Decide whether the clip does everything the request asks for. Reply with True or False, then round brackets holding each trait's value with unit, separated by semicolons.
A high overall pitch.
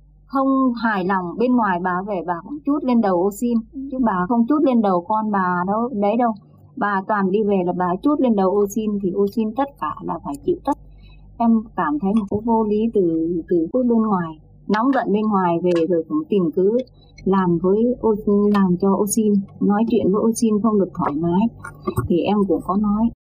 True (205 Hz)